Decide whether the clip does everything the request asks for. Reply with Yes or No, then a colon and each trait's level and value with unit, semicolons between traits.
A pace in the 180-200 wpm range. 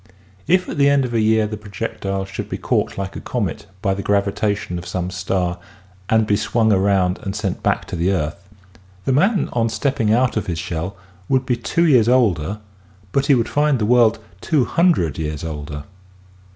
Yes: average, 195 wpm